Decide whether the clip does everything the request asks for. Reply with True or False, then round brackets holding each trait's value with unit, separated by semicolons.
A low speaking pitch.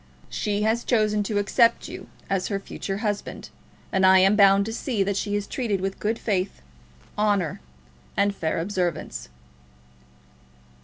False (200 Hz)